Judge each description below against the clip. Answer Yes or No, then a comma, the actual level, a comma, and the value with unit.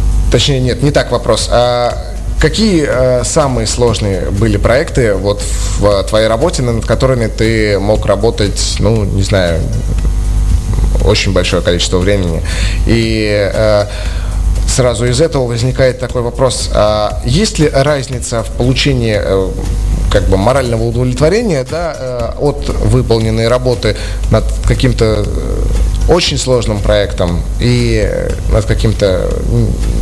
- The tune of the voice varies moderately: Yes, average, 4.1 semitones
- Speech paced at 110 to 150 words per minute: Yes, average, 120 wpm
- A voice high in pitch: No, low, 110 Hz